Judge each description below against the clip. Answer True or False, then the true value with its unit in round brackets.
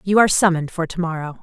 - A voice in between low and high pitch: True (175 Hz)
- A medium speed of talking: False (255 wpm)